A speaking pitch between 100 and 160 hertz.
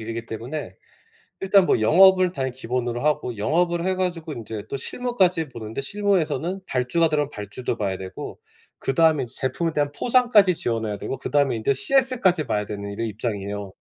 Yes: medium, 140 Hz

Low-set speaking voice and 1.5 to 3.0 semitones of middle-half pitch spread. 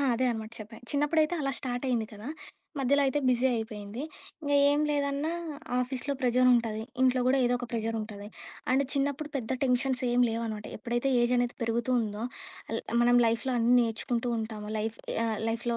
No: high, 245 Hz; average, 2.7 semitones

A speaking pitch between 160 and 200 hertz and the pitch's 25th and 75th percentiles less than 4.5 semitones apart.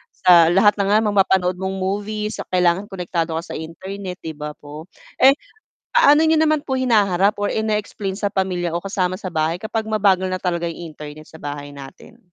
Yes: high, 190 Hz; average, 3.6 semitones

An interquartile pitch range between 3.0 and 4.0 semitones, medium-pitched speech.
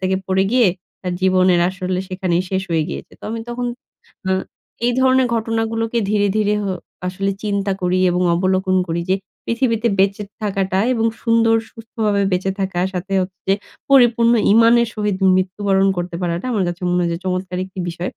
No: average, 3.5 semitones; high, 195 Hz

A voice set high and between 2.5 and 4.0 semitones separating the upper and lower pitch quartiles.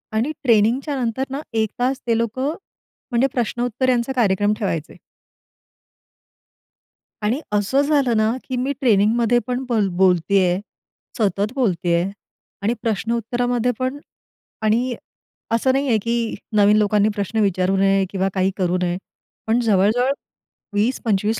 Yes: high, 225 Hz; average, 3.6 semitones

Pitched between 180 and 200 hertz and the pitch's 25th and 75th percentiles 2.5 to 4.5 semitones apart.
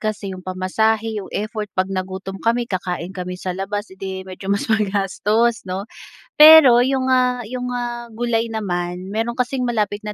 No: high, 210 Hz; average, 3.9 semitones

